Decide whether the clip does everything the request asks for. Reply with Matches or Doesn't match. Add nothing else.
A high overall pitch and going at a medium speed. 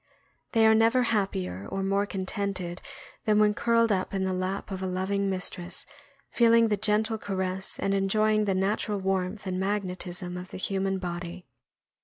Matches